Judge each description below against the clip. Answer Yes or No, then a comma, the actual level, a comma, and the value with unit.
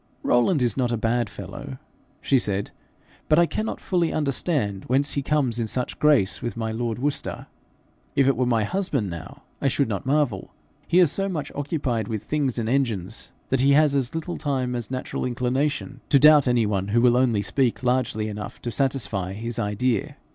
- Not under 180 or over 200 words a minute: Yes, average, 190 wpm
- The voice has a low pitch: Yes, low, 125 Hz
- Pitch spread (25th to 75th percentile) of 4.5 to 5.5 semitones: No, average, 4.0 semitones